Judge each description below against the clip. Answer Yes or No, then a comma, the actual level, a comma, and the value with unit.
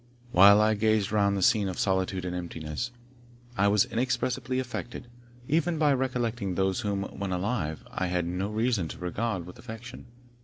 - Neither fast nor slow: Yes, average, 165 wpm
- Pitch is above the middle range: No, low, 105 Hz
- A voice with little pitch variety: No, average, 4.4 semitones